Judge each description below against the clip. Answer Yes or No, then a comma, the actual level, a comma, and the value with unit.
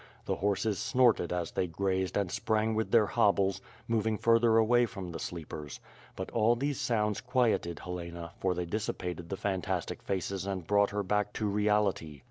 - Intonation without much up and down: No, average, 3.6 semitones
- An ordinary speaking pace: Yes, average, 170 wpm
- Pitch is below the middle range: Yes, low, 100 Hz